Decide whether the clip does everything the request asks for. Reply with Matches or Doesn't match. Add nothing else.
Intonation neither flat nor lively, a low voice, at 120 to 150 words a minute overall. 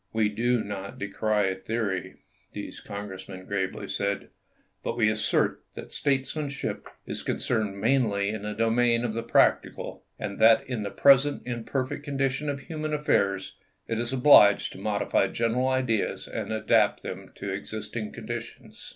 Matches